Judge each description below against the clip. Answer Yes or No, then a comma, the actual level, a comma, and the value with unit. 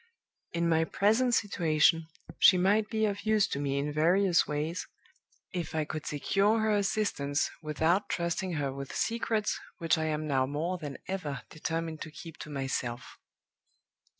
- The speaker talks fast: No, average, 155 wpm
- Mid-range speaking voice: Yes, medium, 165 Hz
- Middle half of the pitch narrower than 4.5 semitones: No, average, 4.8 semitones